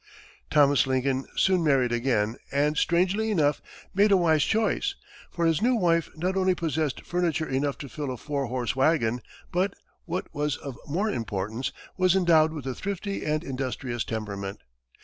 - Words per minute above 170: No, average, 165 wpm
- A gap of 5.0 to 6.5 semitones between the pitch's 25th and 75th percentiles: Yes, average, 5.3 semitones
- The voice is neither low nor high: Yes, medium, 150 Hz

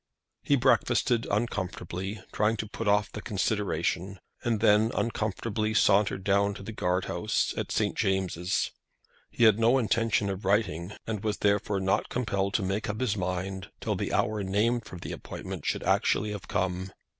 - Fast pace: No, average, 170 wpm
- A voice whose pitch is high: No, low, 100 Hz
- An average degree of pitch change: No, narrow, 2.2 semitones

